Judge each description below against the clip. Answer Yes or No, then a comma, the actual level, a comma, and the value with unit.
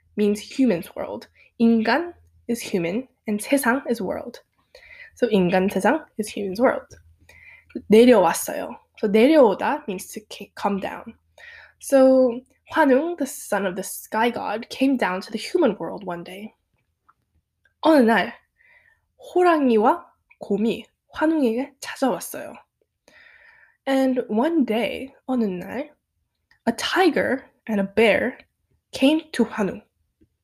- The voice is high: Yes, high, 235 Hz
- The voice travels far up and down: No, average, 4.8 semitones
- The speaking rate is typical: No, slow, 115 wpm